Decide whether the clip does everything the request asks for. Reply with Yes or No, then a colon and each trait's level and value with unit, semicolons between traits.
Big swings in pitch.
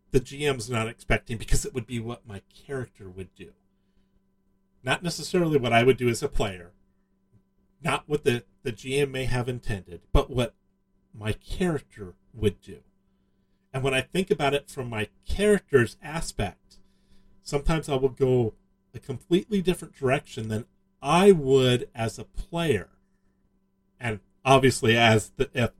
Yes: wide, 5.9 semitones